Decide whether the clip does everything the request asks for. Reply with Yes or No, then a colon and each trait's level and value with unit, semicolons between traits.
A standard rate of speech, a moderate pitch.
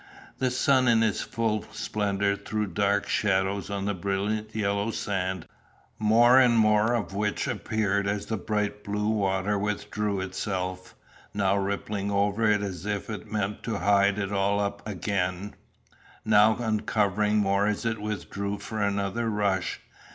No: average, 150 wpm; low, 105 Hz